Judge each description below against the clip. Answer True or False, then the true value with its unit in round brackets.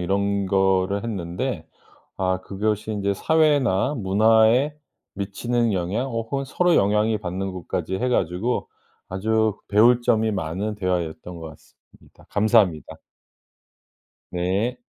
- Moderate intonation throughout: True (3.3 semitones)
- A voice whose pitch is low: True (100 Hz)